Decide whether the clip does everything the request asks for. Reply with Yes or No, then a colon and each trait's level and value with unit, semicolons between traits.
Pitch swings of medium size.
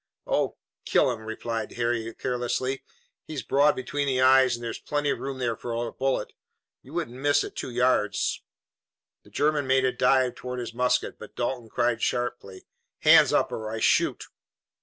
No: narrow, 2.1 semitones